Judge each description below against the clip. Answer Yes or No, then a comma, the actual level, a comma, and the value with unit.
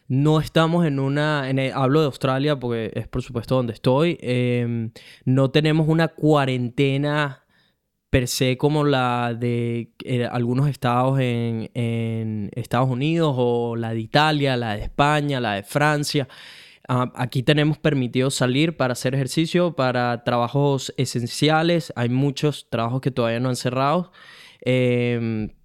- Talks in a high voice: No, low, 130 Hz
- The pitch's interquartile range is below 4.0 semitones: Yes, average, 3.4 semitones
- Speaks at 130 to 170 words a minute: Yes, average, 145 wpm